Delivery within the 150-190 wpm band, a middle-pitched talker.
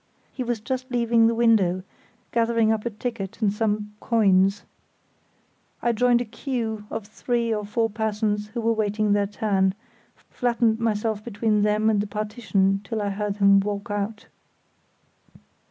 No: average, 155 wpm; high, 215 Hz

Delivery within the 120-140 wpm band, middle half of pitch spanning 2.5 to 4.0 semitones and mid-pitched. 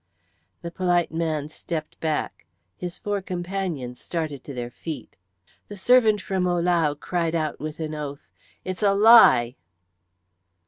Yes: slow, 135 wpm; average, 3.7 semitones; medium, 170 Hz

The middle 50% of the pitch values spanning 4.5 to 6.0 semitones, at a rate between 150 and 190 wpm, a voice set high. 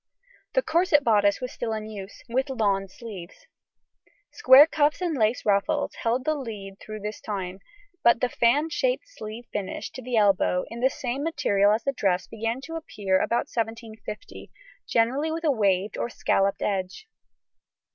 Yes: average, 5.1 semitones; average, 165 wpm; high, 230 Hz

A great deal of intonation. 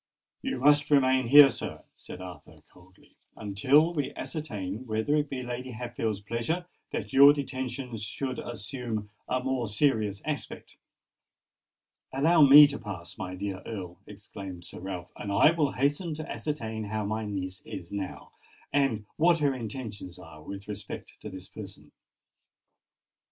Yes: wide, 5.8 semitones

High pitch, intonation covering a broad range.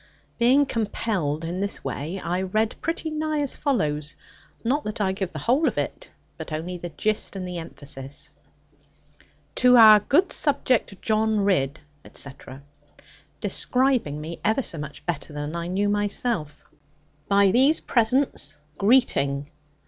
Yes: high, 200 Hz; wide, 7.6 semitones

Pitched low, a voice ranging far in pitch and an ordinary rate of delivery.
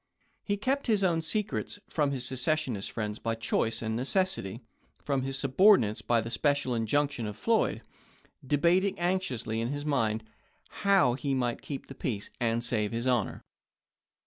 Yes: low, 130 Hz; wide, 6.2 semitones; average, 160 wpm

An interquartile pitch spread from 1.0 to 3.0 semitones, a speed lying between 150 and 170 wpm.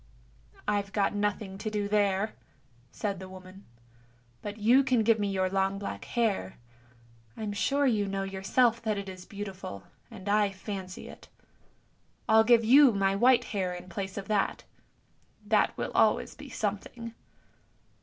Yes: narrow, 2.4 semitones; average, 160 wpm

